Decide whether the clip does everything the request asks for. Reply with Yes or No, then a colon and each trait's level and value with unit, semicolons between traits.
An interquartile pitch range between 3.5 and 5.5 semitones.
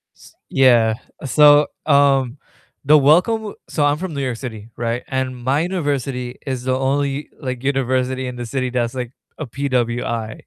No: narrow, 2.6 semitones